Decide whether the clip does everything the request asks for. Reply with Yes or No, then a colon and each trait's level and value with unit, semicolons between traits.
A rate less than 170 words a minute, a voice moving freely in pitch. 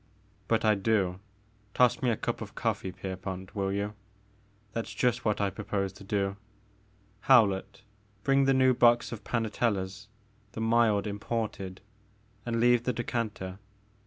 No: average, 160 wpm; average, 2.9 semitones